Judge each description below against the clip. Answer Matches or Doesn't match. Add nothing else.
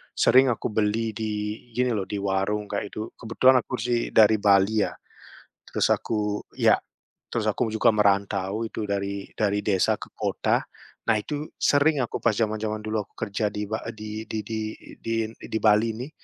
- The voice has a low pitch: Matches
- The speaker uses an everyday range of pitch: Doesn't match